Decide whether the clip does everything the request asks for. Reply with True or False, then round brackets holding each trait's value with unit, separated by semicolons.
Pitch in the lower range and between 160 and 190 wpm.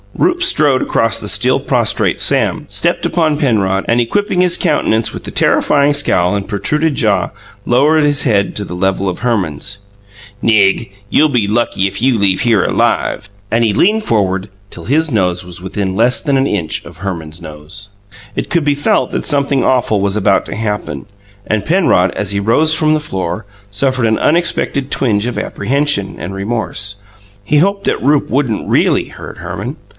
True (110 Hz; 180 wpm)